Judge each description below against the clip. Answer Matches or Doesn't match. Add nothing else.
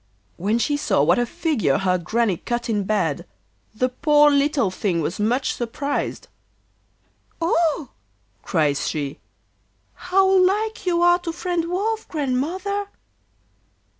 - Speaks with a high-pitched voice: Matches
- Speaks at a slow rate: Matches